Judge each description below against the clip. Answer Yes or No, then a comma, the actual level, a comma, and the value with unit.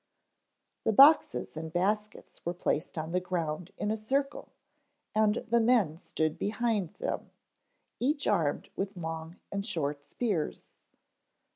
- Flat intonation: No, wide, 5.4 semitones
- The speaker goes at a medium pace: No, slow, 130 wpm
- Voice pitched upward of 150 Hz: Yes, high, 190 Hz